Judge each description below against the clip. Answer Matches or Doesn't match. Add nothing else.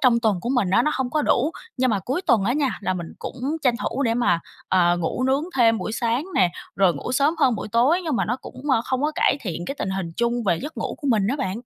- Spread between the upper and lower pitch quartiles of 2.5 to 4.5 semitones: Doesn't match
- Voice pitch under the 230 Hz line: Doesn't match